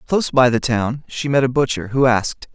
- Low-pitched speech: Yes, low, 125 Hz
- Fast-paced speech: Yes, fast, 235 wpm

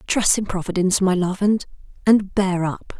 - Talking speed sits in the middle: Yes, average, 160 wpm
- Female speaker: Yes, female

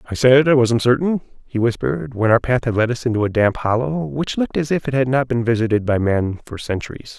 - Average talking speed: No, fast, 250 wpm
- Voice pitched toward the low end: Yes, low, 120 Hz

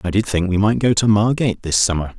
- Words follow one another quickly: Yes, fast, 275 wpm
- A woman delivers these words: No, male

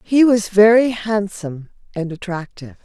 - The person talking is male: No, female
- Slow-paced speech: Yes, slow, 125 wpm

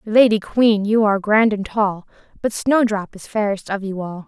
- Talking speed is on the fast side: No, average, 195 wpm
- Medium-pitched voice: No, high, 210 Hz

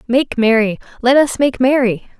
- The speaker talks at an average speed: Yes, average, 165 wpm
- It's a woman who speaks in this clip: Yes, female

